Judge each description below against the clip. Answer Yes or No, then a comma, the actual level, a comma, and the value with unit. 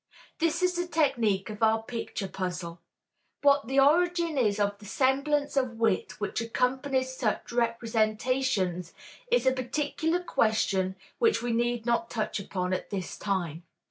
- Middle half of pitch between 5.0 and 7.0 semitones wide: Yes, average, 5.3 semitones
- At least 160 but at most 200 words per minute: No, average, 145 wpm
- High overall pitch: Yes, high, 235 Hz